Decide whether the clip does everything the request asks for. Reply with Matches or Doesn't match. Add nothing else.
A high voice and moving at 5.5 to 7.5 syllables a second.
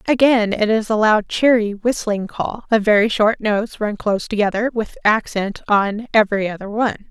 Doesn't match